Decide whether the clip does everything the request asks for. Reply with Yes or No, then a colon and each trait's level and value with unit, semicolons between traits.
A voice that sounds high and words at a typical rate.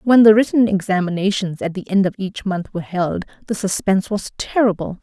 Yes: high, 195 Hz; average, 190 wpm